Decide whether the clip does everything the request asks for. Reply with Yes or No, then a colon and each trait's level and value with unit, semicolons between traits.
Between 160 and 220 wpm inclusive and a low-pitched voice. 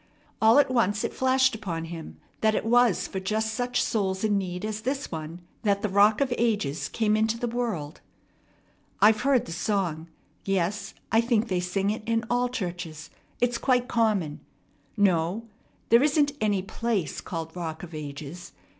No: average, 170 wpm; high, 210 Hz